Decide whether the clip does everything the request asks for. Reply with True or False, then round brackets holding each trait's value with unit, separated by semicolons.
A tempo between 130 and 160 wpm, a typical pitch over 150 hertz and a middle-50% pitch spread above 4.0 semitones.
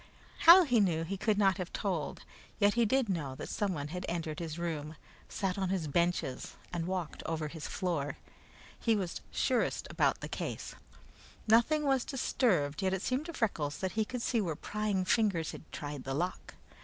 False (185 wpm; 185 Hz; 5.1 semitones)